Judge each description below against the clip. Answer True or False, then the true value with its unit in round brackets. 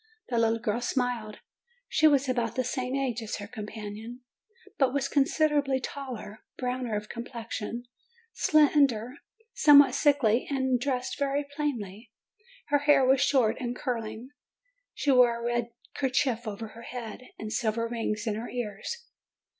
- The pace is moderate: True (145 wpm)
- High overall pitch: True (245 Hz)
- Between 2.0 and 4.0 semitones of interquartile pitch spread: True (3.4 semitones)